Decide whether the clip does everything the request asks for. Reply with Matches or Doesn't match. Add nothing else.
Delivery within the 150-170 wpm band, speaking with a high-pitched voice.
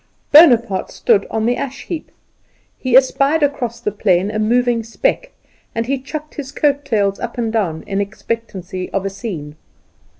Matches